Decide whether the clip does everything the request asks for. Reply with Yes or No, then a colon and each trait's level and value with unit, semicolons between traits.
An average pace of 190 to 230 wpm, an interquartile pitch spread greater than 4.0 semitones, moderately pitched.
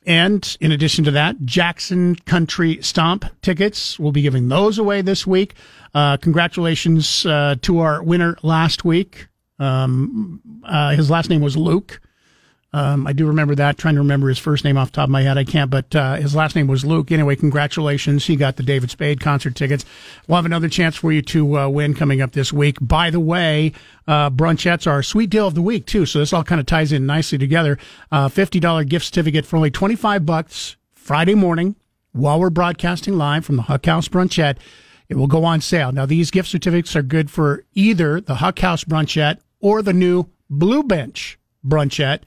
No: fast, 205 wpm; average, 3.4 semitones; medium, 160 Hz